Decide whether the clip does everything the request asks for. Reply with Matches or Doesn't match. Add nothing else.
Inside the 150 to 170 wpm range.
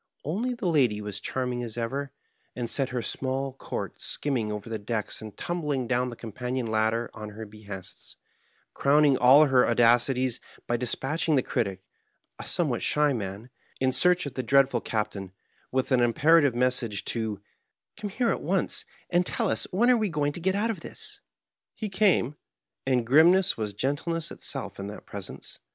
Doesn't match